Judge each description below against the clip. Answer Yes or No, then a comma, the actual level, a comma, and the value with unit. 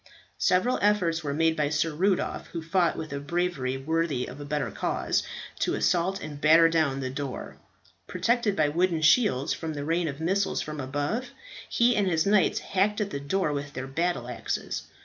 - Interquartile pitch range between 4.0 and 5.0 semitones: Yes, average, 4.4 semitones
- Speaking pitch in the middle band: Yes, medium, 160 Hz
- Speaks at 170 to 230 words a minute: Yes, average, 190 wpm